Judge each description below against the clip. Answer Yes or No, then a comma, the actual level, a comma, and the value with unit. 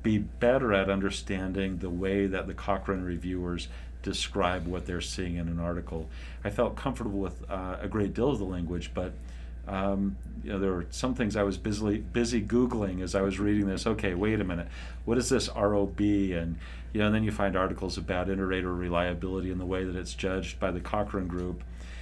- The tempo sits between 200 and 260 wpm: Yes, fast, 205 wpm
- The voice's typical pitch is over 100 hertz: No, very low, 95 Hz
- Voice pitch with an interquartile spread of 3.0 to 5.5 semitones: No, narrow, 2.5 semitones